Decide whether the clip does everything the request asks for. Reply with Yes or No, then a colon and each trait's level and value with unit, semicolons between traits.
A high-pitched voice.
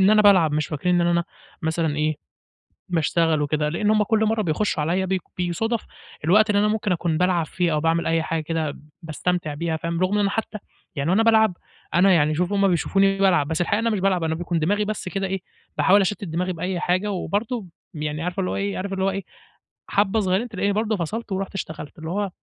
No: medium, 180 Hz